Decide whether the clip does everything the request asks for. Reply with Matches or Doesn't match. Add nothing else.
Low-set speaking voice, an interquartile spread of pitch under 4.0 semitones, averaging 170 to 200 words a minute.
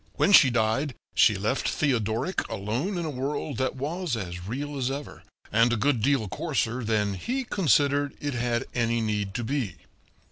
Doesn't match